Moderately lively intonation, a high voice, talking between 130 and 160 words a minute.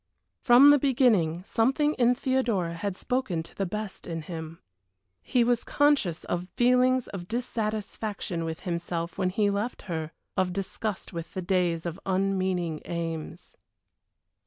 No: wide, 5.9 semitones; high, 195 Hz; average, 140 wpm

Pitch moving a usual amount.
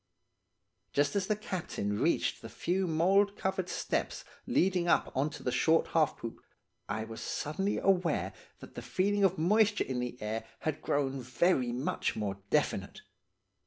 No: wide, 7.4 semitones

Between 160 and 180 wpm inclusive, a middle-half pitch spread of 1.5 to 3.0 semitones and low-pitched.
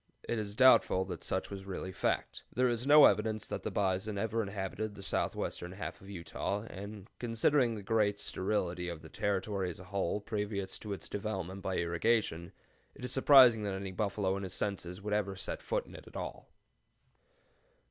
No: average, 190 wpm; narrow, 2.5 semitones; low, 100 Hz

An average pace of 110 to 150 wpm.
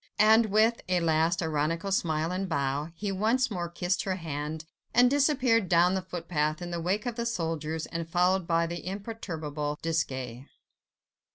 No: average, 165 wpm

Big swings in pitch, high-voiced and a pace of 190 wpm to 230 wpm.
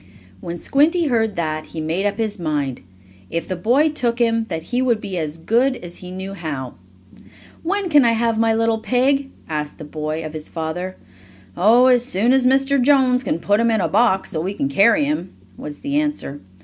Yes: wide, 7.4 semitones; high, 220 Hz; fast, 205 wpm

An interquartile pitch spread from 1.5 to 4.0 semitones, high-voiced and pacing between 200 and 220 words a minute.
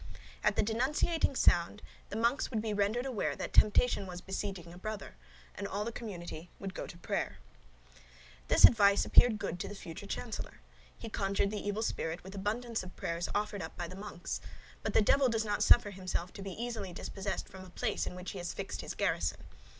Yes: average, 3.3 semitones; high, 200 Hz; fast, 205 wpm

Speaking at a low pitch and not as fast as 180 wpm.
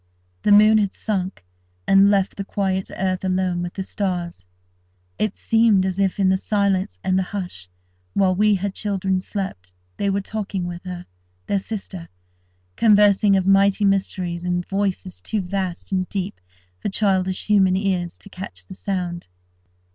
No: high, 190 Hz; average, 155 wpm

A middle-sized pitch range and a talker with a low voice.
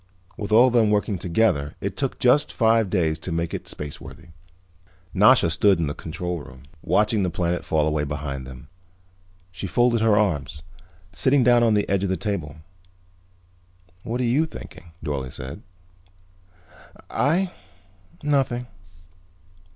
No: wide, 6.6 semitones; very low, 95 Hz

